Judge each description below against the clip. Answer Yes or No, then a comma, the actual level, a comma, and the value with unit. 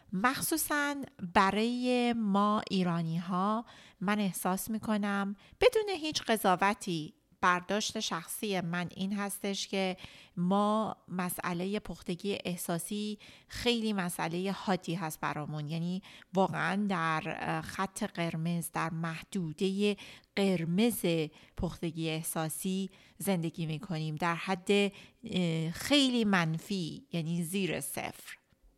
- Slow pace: Yes, slow, 100 wpm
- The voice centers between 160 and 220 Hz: Yes, high, 190 Hz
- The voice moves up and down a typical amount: Yes, average, 3.4 semitones